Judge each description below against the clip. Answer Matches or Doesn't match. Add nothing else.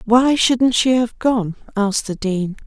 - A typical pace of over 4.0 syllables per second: Doesn't match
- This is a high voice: Matches